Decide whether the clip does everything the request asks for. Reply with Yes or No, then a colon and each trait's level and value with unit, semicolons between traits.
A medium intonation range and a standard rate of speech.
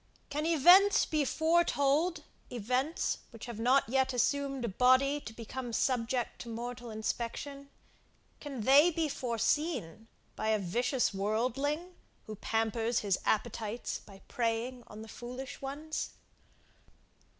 No: average, 4.0 semitones; slow, 125 wpm